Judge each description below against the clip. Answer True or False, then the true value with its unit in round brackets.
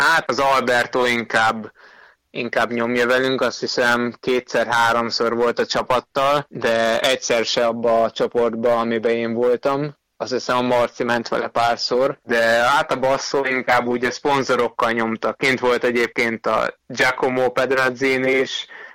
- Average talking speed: True (145 wpm)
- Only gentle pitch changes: True (2.2 semitones)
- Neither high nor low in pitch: False (120 Hz)